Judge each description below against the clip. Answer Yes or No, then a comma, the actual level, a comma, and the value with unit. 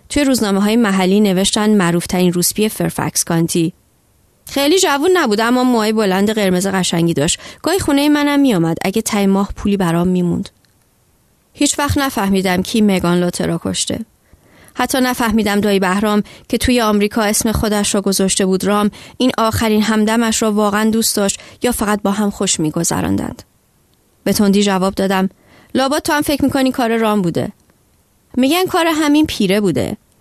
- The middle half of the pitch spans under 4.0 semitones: No, average, 4.3 semitones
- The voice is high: Yes, high, 210 Hz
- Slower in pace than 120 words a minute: No, fast, 155 wpm